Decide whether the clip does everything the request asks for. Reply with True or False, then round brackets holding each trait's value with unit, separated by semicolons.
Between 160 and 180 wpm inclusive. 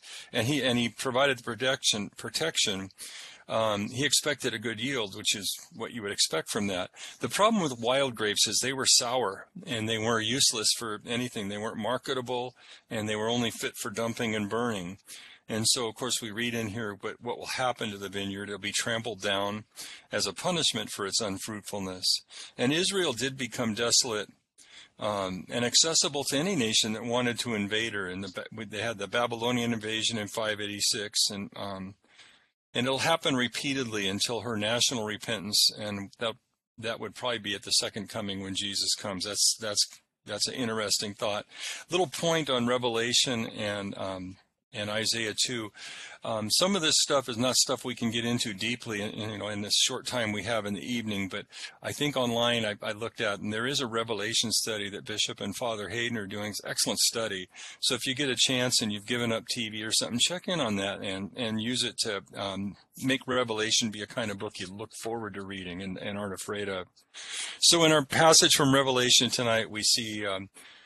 False (205 wpm)